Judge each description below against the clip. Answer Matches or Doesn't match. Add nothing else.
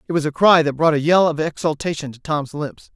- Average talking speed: Doesn't match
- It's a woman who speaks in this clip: Doesn't match